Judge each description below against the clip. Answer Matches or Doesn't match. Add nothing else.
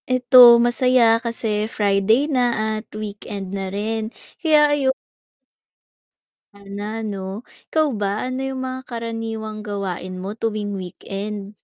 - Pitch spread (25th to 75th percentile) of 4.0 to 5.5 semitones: Doesn't match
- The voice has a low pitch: Doesn't match